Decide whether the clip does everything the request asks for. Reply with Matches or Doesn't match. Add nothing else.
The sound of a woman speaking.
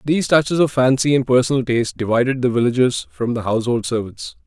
Doesn't match